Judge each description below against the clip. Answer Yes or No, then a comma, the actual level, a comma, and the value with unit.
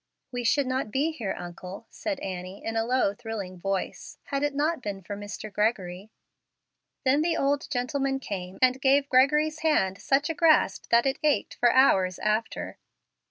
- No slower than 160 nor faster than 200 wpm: Yes, average, 170 wpm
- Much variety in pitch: Yes, wide, 5.9 semitones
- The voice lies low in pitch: No, high, 245 Hz